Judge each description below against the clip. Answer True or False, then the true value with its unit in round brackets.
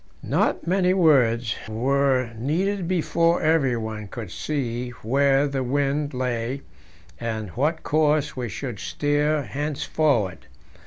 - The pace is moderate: False (110 wpm)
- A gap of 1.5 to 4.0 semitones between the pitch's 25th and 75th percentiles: False (4.4 semitones)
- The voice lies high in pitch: False (140 Hz)